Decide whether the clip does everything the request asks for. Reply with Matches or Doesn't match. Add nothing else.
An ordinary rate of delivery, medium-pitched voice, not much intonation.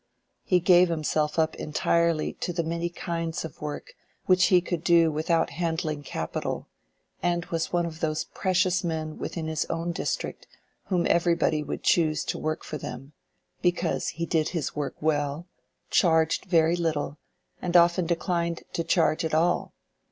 Matches